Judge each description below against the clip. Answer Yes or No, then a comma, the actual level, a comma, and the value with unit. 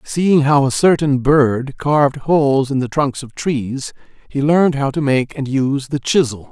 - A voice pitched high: No, medium, 140 Hz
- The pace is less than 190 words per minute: No, average, 195 wpm